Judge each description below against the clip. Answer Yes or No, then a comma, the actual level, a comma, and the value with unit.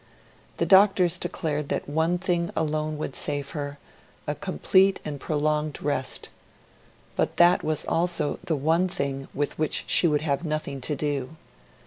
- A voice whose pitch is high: No, medium, 155 Hz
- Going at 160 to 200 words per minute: No, average, 150 wpm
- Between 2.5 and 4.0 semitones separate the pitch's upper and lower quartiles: Yes, average, 2.9 semitones